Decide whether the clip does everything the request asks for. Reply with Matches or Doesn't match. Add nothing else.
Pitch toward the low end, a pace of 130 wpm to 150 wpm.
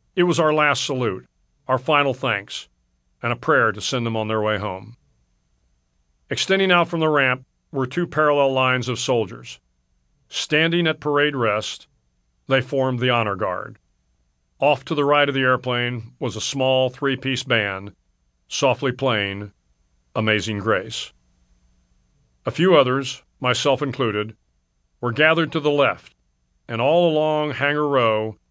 Matches